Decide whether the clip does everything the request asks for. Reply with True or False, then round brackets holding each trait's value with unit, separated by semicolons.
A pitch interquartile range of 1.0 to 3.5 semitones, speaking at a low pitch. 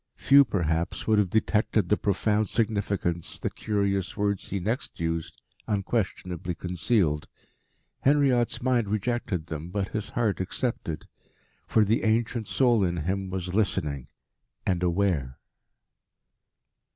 False (4.0 semitones; 100 Hz)